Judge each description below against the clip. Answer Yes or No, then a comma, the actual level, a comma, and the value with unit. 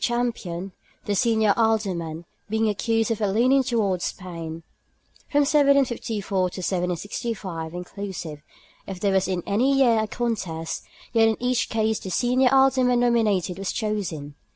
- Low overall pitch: No, high, 210 Hz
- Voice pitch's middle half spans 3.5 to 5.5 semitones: Yes, average, 4.7 semitones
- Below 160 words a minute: Yes, average, 140 wpm